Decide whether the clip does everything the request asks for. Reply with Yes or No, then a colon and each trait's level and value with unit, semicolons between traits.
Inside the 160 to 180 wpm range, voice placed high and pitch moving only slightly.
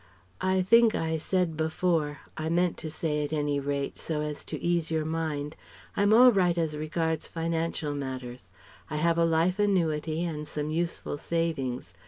No: average, 170 wpm; medium, 160 Hz; narrow, 2.3 semitones